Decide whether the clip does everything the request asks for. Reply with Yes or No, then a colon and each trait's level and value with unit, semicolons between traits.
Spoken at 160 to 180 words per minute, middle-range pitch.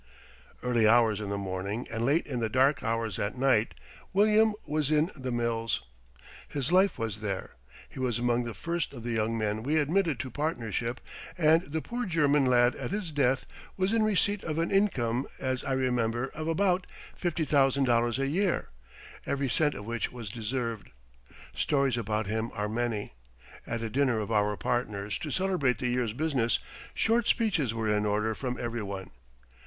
No: average, 175 wpm; low, 125 Hz